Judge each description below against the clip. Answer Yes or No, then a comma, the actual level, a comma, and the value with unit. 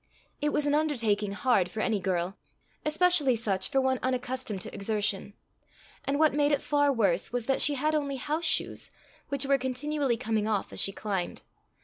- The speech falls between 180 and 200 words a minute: Yes, average, 185 wpm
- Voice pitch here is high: Yes, very high, 255 Hz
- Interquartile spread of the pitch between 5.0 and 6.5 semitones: Yes, wide, 5.6 semitones